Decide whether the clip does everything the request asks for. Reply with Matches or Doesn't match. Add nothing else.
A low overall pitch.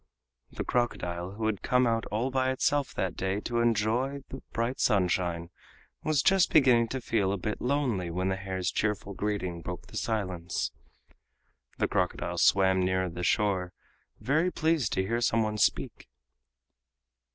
Matches